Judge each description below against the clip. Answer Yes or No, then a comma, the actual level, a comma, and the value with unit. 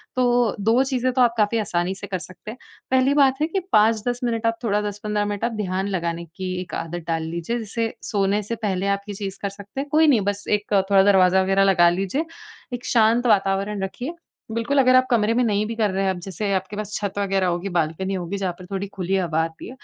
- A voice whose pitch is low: No, high, 205 Hz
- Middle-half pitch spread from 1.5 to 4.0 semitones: Yes, average, 3.4 semitones